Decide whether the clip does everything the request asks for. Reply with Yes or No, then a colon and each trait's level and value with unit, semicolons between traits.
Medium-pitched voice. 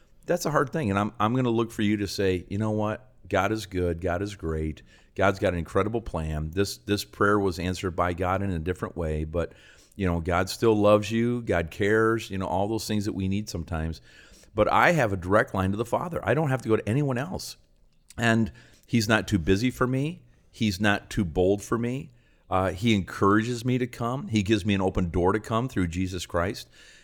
No: low, 100 Hz